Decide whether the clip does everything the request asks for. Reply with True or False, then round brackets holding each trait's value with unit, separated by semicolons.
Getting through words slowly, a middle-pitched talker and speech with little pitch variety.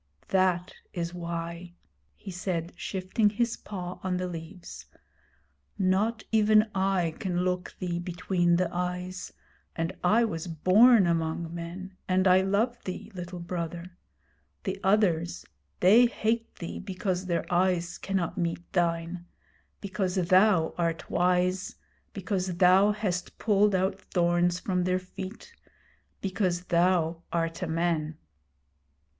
True (125 wpm; 180 Hz; 1.9 semitones)